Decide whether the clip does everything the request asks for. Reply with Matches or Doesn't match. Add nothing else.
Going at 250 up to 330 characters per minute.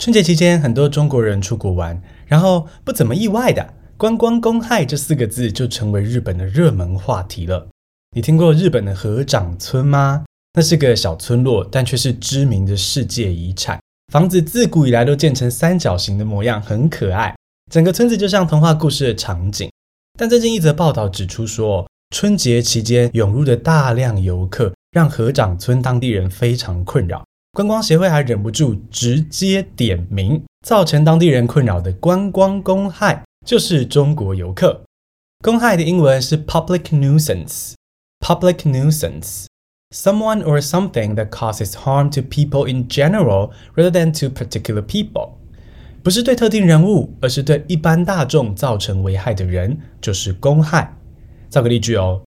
Doesn't match